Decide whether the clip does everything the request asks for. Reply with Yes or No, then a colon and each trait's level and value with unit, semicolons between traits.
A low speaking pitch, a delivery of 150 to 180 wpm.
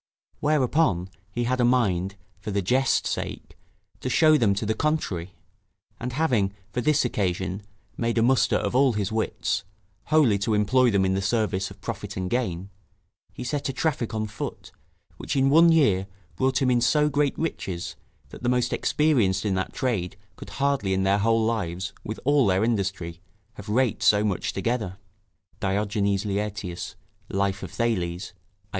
Yes: low, 110 Hz; average, 170 wpm